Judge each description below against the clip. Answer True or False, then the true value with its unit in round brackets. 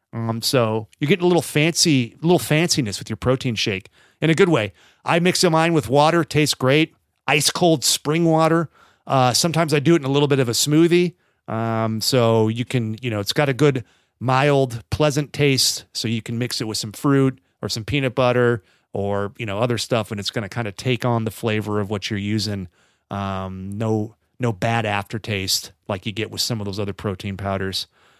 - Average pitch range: False (5.8 semitones)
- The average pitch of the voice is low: True (120 Hz)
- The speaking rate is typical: False (210 wpm)